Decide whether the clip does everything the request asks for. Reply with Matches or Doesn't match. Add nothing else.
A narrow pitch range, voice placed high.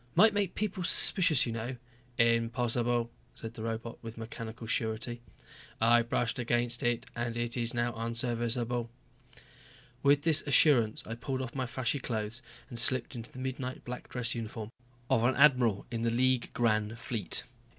Doesn't match